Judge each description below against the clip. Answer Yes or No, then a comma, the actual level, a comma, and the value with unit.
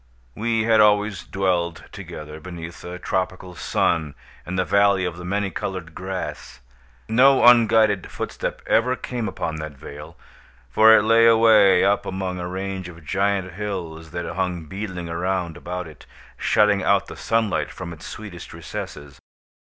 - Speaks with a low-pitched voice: Yes, very low, 95 Hz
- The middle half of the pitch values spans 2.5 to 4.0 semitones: Yes, average, 3.3 semitones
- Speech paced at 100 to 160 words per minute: Yes, average, 150 wpm